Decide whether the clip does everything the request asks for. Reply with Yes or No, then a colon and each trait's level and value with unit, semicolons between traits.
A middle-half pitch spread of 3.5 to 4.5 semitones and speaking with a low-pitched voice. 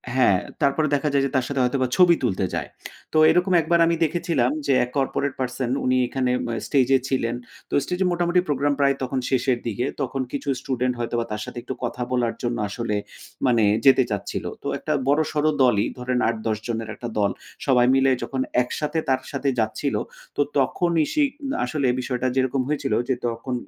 No: average, 2.9 semitones; low, 130 Hz